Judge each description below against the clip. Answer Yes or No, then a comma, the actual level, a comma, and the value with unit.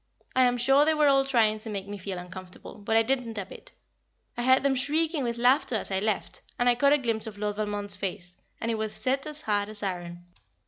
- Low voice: No, high, 225 Hz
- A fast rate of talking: Yes, fast, 240 wpm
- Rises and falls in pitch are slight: No, average, 4.6 semitones